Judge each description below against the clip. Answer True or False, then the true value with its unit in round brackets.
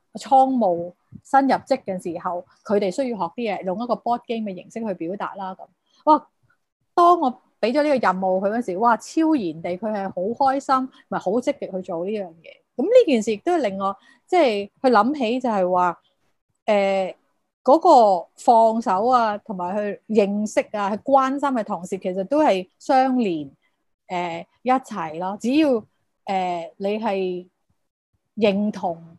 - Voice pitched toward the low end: False (215 Hz)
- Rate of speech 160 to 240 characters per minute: False (250 characters per minute)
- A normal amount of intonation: False (5.8 semitones)